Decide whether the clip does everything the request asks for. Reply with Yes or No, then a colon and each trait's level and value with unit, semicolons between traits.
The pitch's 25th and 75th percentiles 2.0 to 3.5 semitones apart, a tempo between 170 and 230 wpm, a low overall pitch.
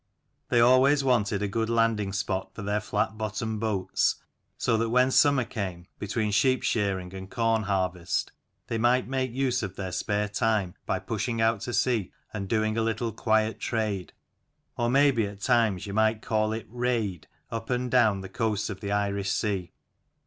Yes: average, 2.8 semitones; average, 185 wpm; low, 110 Hz